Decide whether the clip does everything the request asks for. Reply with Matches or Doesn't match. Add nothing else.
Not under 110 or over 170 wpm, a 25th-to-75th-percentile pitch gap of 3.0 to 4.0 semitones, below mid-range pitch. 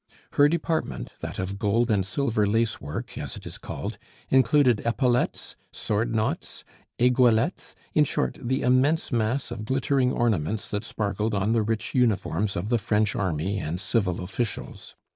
Matches